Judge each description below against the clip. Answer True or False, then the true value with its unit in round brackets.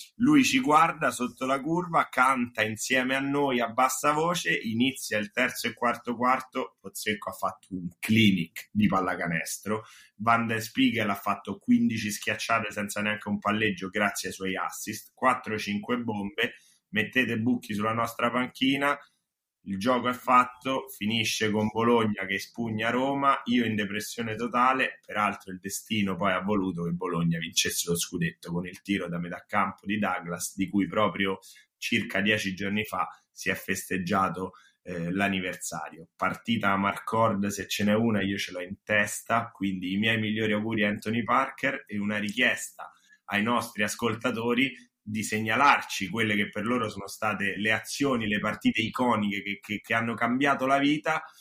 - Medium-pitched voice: False (110 Hz)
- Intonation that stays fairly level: False (3.5 semitones)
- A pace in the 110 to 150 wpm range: False (160 wpm)